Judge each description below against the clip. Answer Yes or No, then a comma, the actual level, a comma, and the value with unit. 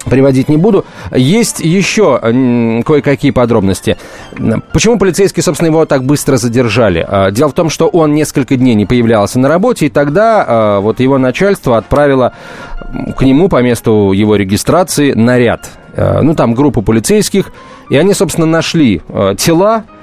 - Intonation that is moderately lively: No, wide, 6.0 semitones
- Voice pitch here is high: No, low, 135 Hz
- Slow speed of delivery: No, average, 140 wpm